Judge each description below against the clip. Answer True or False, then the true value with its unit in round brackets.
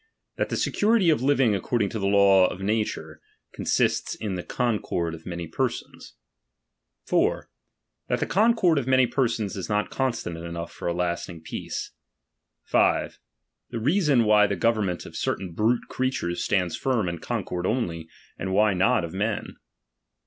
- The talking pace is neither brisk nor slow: True (155 wpm)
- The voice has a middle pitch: False (105 Hz)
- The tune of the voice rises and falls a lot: True (5.9 semitones)